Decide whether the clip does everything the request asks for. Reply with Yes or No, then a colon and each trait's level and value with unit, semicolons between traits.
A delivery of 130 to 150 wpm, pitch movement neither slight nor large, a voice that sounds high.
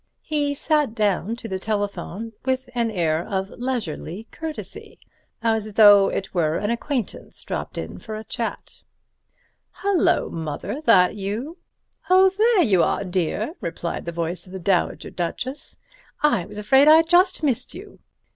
No: average, 145 wpm; wide, 7.2 semitones; high, 220 Hz